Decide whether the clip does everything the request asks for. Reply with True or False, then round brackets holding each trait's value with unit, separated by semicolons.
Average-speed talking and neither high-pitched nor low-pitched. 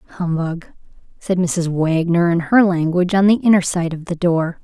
True (180 wpm; 175 Hz)